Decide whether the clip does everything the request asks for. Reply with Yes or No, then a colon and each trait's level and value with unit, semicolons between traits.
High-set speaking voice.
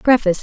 Yes: high, 220 Hz